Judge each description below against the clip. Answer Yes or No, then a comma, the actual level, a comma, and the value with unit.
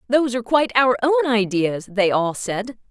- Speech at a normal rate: Yes, average, 185 wpm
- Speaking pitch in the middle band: No, high, 235 Hz